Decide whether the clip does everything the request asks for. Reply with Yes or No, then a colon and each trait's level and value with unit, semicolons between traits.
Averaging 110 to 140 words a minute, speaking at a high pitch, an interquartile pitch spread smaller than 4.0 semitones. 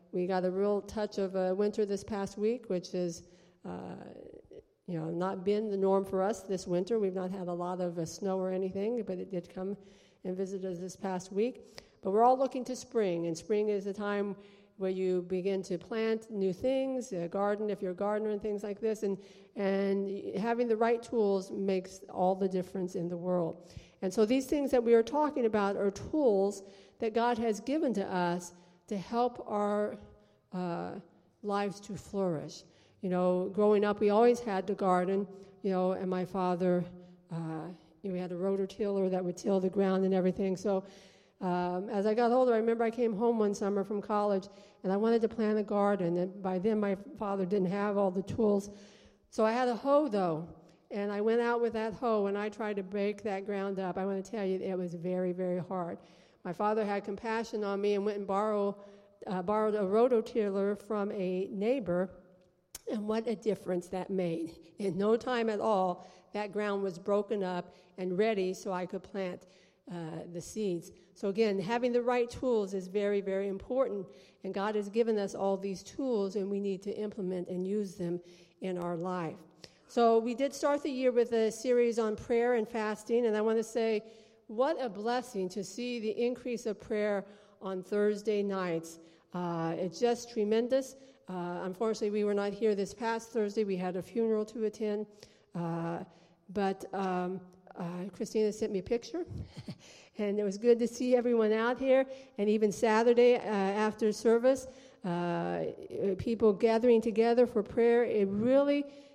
No: average, 195 wpm; high, 200 Hz; average, 3.2 semitones